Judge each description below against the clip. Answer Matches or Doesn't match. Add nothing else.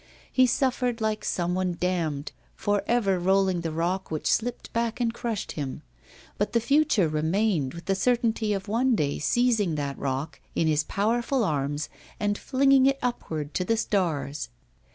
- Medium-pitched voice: Doesn't match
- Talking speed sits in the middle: Matches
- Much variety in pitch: Matches